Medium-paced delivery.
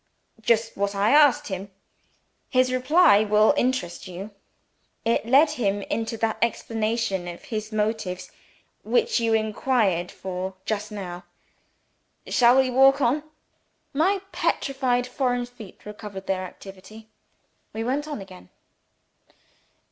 No: slow, 120 wpm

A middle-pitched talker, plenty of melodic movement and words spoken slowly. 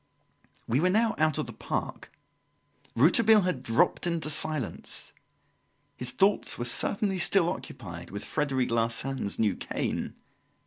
Yes: medium, 145 Hz; wide, 7.6 semitones; slow, 130 wpm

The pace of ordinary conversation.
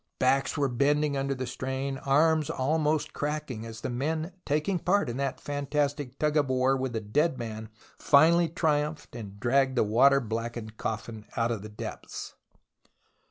Yes: average, 160 wpm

